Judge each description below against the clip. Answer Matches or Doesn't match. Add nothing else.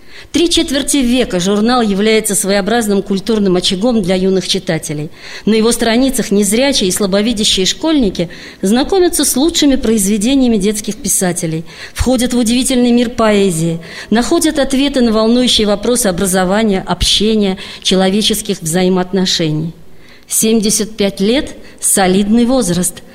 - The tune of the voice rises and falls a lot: Doesn't match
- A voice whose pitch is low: Doesn't match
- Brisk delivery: Doesn't match